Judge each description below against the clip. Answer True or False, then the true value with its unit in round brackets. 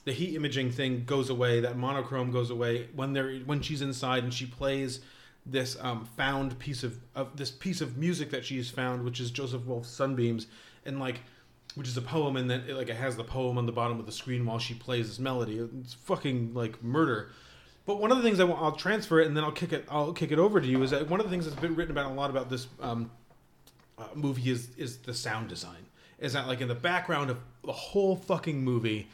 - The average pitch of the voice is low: True (130 Hz)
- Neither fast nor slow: False (245 wpm)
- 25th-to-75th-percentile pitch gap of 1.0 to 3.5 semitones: True (3.2 semitones)